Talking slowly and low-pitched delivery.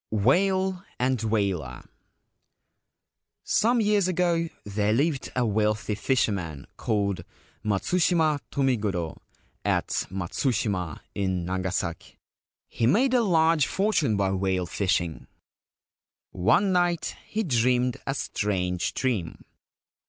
Yes: slow, 100 wpm; low, 115 Hz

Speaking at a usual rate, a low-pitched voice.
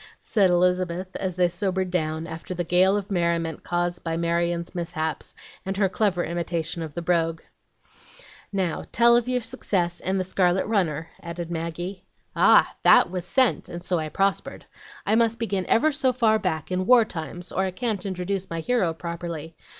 No: average, 175 wpm; medium, 180 Hz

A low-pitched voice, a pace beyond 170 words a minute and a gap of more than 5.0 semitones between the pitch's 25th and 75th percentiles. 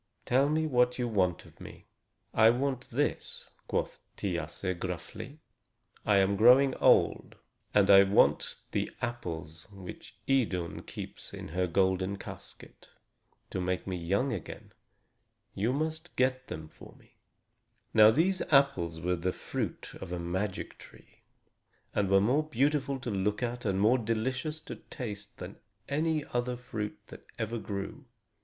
No: low, 110 Hz; average, 145 wpm; wide, 5.6 semitones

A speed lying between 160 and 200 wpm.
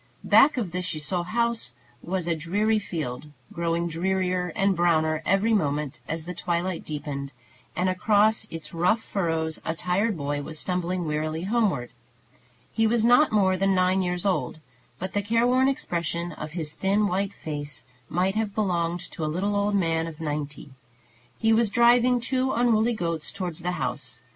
Yes: average, 165 wpm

